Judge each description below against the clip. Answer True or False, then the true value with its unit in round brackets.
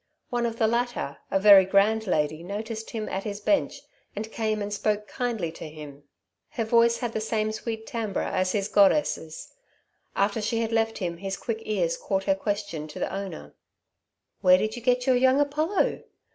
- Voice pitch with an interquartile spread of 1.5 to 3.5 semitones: True (3.1 semitones)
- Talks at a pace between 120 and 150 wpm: False (185 wpm)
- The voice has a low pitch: False (215 Hz)